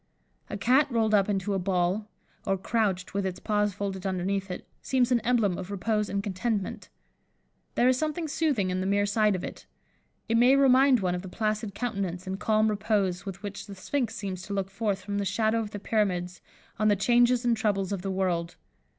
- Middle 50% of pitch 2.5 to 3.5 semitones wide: Yes, average, 3.0 semitones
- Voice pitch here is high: Yes, high, 205 Hz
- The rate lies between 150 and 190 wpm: No, fast, 205 wpm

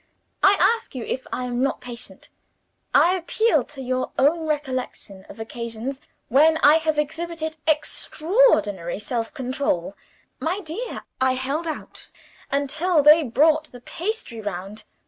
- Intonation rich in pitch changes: No, average, 4.7 semitones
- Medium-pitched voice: No, very high, 280 Hz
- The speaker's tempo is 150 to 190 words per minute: No, slow, 135 wpm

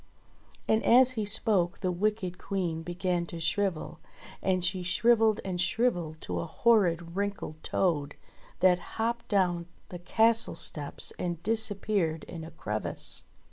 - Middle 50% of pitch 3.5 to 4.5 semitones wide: Yes, average, 3.9 semitones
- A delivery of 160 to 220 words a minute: No, average, 140 wpm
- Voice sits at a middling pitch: Yes, medium, 180 Hz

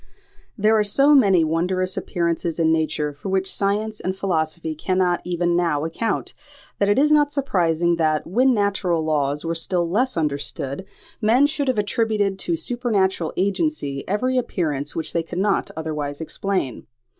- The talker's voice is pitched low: No, medium, 180 Hz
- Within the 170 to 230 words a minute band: No, average, 155 wpm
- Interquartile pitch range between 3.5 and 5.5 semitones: Yes, average, 4.5 semitones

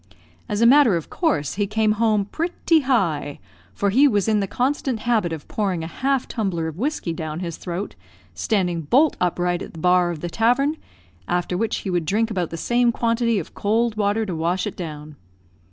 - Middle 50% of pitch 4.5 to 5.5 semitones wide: Yes, average, 5.2 semitones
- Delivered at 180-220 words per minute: Yes, average, 200 wpm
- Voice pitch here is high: Yes, high, 205 Hz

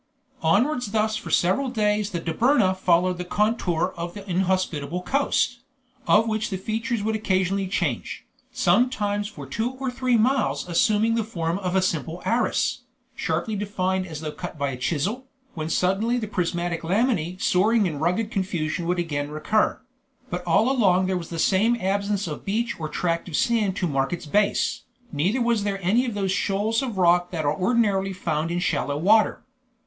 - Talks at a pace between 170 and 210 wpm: Yes, average, 175 wpm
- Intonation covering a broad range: No, average, 4.2 semitones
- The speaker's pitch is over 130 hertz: Yes, high, 190 Hz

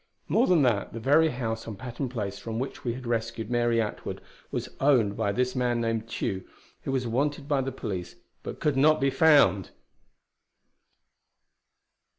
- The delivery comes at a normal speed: Yes, average, 165 wpm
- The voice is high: No, low, 120 Hz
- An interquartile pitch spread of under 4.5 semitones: Yes, average, 3.2 semitones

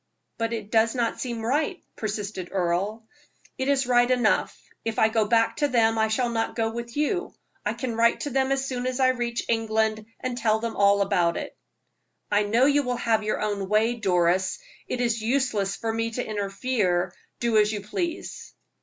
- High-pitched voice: Yes, high, 225 Hz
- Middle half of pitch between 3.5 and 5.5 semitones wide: No, average, 2.7 semitones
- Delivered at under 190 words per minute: No, average, 195 wpm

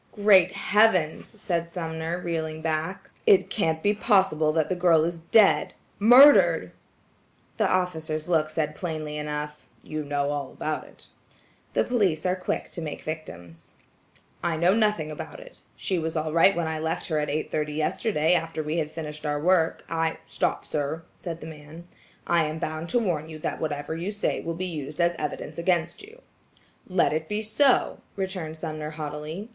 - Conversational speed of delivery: Yes, average, 170 wpm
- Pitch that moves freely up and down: No, average, 3.0 semitones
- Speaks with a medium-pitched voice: Yes, medium, 160 Hz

